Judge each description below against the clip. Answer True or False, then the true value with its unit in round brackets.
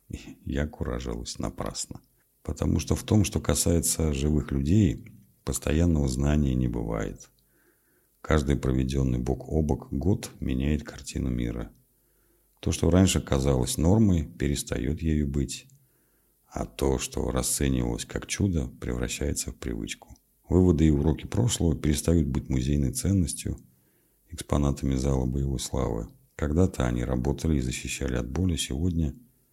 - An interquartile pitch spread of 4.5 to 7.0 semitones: False (3.9 semitones)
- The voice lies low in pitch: True (70 Hz)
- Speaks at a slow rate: False (125 wpm)